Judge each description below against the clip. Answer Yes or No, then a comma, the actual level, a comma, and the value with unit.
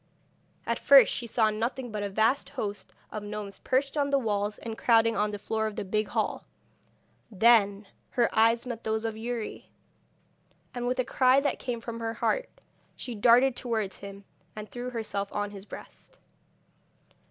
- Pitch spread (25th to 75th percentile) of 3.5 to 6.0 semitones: No, average, 2.7 semitones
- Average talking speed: Yes, average, 175 wpm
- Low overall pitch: No, high, 225 Hz